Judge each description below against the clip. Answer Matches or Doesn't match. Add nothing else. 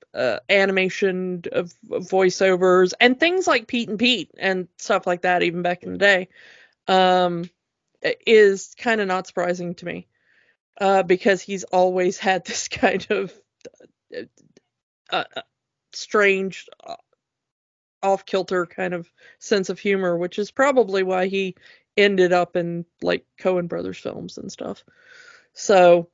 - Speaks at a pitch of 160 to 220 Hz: Matches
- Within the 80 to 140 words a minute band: Matches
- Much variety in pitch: Doesn't match